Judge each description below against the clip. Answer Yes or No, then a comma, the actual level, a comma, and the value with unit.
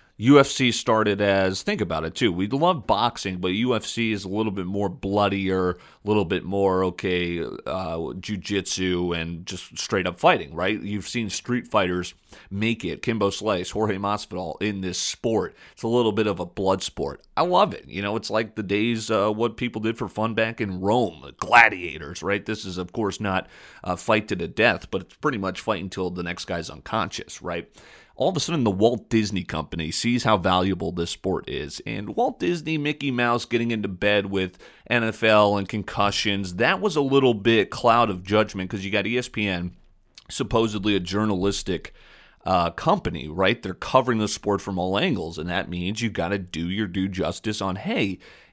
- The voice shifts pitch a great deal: No, average, 3.3 semitones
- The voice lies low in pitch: Yes, low, 100 Hz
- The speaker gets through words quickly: No, average, 195 wpm